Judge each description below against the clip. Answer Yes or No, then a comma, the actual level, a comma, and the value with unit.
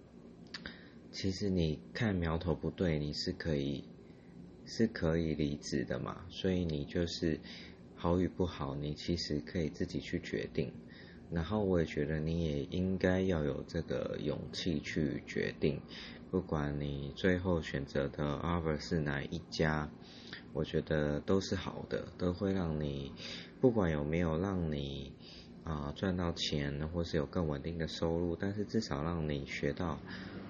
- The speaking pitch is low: Yes, very low, 80 Hz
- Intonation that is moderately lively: Yes, average, 3.6 semitones